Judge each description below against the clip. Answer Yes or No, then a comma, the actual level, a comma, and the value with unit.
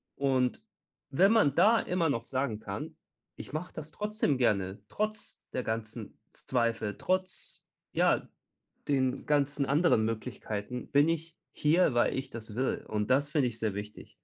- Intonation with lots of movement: Yes, wide, 5.7 semitones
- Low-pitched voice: Yes, low, 130 Hz